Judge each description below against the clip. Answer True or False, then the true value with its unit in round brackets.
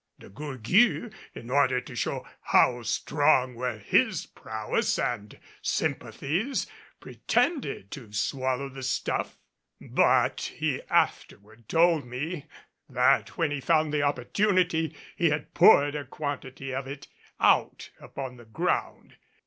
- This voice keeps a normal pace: False (125 wpm)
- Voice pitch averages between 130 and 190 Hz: True (135 Hz)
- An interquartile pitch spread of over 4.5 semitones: False (3.8 semitones)